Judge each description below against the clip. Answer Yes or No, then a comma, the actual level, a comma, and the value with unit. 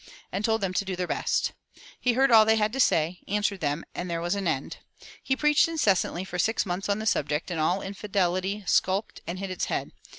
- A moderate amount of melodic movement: Yes, average, 3.5 semitones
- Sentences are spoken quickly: Yes, fast, 225 wpm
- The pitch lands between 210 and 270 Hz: No, high, 195 Hz